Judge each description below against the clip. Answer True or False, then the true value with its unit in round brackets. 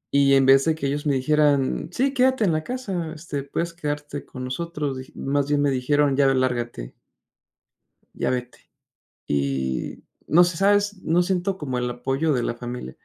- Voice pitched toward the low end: False (145 Hz)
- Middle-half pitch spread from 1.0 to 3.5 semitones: False (4.6 semitones)